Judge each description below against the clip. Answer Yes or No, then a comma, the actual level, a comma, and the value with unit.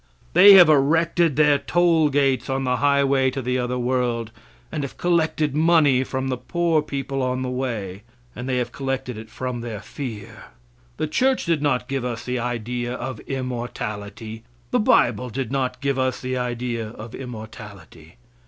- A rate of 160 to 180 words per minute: Yes, average, 170 wpm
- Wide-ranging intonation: No, average, 2.7 semitones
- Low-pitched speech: Yes, low, 130 Hz